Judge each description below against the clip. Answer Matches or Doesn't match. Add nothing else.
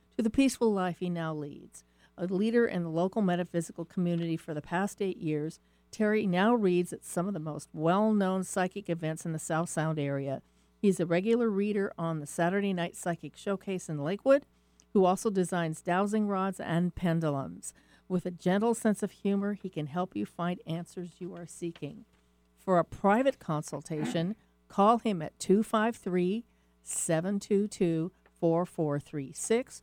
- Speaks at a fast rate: Doesn't match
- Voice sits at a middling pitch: Matches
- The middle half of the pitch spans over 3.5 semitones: Matches